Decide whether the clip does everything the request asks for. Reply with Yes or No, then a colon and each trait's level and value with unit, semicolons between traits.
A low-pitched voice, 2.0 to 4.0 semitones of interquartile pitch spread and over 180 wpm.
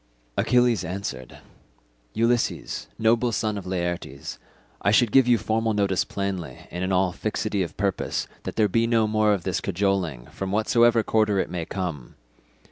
No: low, 100 Hz; average, 3.4 semitones; average, 160 wpm